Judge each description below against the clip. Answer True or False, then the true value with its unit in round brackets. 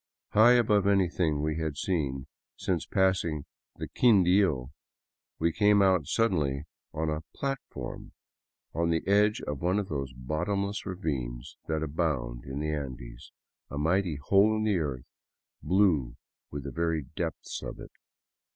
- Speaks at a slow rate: False (150 wpm)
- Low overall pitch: True (80 Hz)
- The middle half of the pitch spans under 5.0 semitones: False (5.4 semitones)